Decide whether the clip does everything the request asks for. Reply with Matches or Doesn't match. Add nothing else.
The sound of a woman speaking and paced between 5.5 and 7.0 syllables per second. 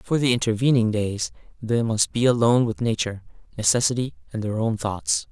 Doesn't match